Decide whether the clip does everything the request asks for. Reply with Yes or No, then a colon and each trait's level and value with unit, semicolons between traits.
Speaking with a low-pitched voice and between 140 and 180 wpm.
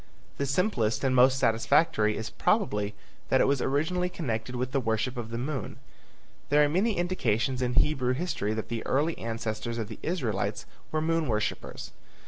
Yes: low, 130 Hz; average, 170 wpm